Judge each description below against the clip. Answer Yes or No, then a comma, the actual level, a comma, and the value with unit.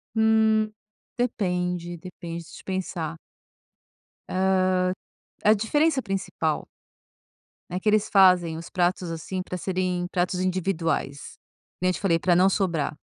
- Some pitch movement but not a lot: No, narrow, 2.1 semitones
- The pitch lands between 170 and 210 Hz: Yes, medium, 185 Hz